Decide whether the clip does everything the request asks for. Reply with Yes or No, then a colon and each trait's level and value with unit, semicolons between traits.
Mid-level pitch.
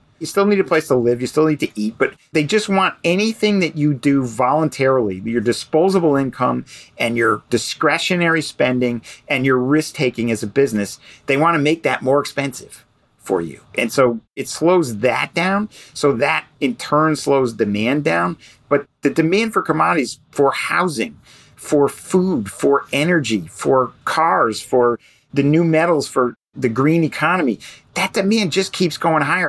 Yes: medium, 145 Hz